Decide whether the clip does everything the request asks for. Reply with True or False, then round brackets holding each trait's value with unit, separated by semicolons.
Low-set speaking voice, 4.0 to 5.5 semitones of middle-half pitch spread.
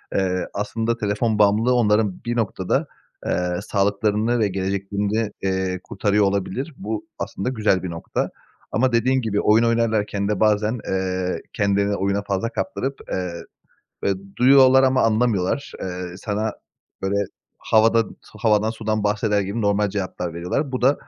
False (105 Hz; 2.7 semitones)